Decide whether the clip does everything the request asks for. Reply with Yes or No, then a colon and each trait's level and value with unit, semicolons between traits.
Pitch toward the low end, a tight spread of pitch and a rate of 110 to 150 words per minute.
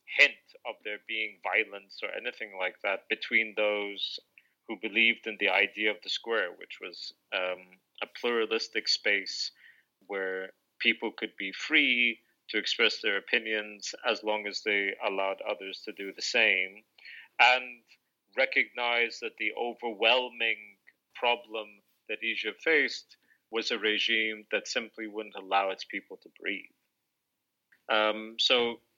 Yes: low, 110 Hz; narrow, 2.2 semitones; slow, 135 wpm